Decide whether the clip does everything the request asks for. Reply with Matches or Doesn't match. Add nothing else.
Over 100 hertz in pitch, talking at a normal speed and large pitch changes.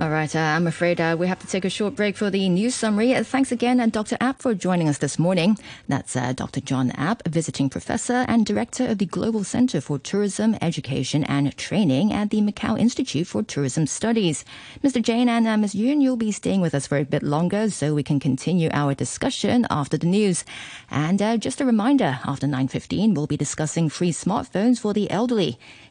Doesn't match